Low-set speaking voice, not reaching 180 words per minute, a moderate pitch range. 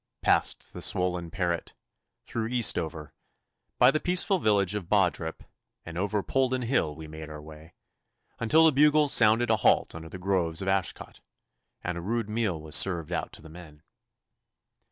No: very low, 95 Hz; average, 165 wpm; wide, 6.2 semitones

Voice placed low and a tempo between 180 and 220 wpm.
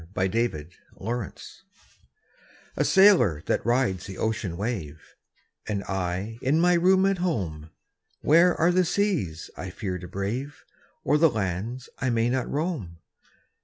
No: low, 115 Hz; slow, 135 wpm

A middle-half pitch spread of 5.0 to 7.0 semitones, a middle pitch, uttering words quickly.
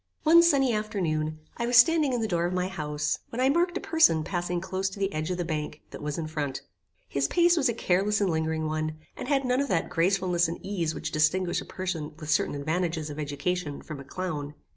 Yes: wide, 5.4 semitones; medium, 175 Hz; fast, 230 wpm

